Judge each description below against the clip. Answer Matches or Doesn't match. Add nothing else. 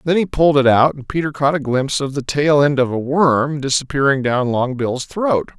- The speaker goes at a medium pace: Doesn't match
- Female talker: Doesn't match